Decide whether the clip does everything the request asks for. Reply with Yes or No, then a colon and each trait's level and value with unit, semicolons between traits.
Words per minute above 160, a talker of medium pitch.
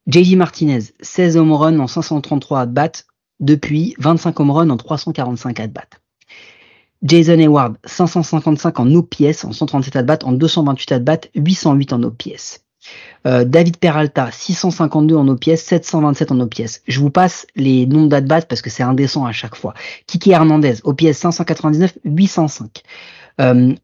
No: slow, 145 wpm; medium, 155 Hz